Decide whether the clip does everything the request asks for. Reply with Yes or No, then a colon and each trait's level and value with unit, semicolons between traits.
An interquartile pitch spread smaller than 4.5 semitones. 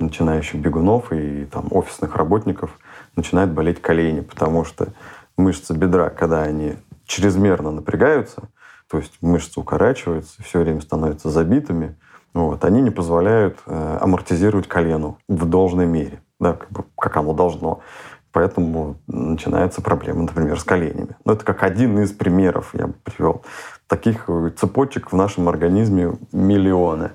Yes: average, 3.2 semitones